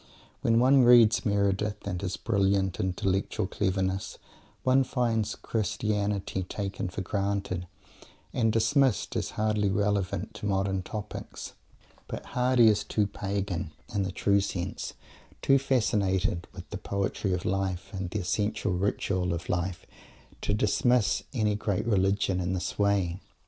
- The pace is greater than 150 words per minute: No, average, 140 wpm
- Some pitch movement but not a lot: No, narrow, 2.2 semitones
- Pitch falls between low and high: No, low, 100 Hz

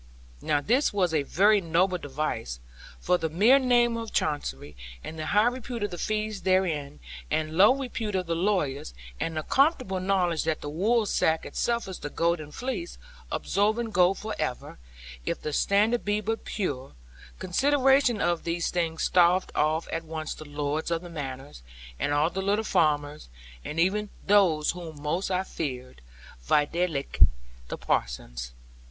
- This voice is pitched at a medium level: Yes, medium, 175 Hz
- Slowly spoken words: No, average, 160 wpm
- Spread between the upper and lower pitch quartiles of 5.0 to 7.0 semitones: Yes, wide, 5.4 semitones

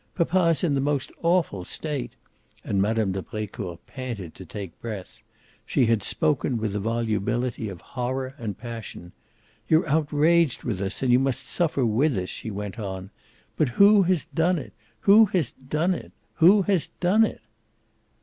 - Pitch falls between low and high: No, low, 125 Hz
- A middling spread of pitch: No, wide, 7.5 semitones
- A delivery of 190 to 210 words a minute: No, average, 165 wpm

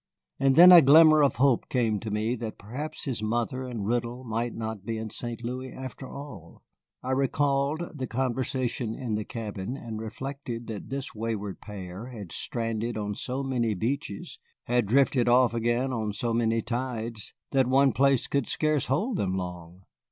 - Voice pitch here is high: No, low, 120 Hz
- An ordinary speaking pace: Yes, average, 175 wpm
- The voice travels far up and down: No, average, 3.3 semitones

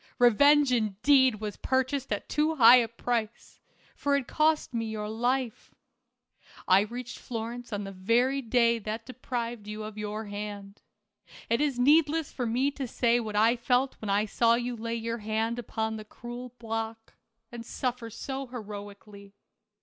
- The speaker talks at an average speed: Yes, average, 165 wpm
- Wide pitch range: No, average, 2.7 semitones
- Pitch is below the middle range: No, high, 230 Hz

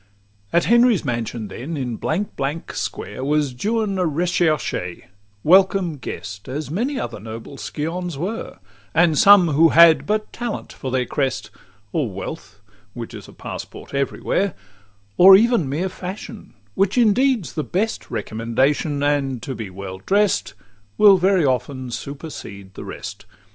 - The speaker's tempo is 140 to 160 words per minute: Yes, average, 150 wpm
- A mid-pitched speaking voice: Yes, medium, 155 Hz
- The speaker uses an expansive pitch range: Yes, wide, 7.1 semitones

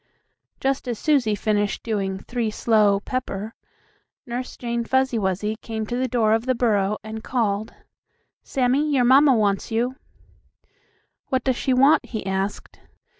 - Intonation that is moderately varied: Yes, average, 3.4 semitones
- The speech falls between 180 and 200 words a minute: No, average, 145 wpm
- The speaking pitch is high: Yes, high, 230 Hz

